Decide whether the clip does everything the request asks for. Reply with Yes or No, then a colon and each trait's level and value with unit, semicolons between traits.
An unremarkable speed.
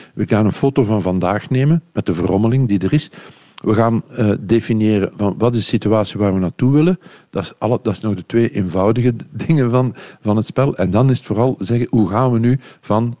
No: fast, 220 wpm